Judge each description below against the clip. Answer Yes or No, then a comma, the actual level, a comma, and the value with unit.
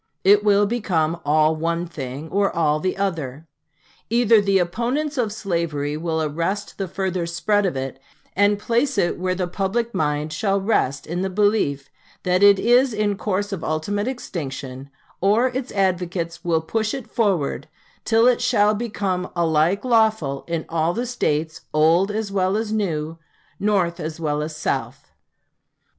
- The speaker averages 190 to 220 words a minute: No, average, 160 wpm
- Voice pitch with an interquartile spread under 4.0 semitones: No, average, 4.8 semitones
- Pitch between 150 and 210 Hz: Yes, medium, 185 Hz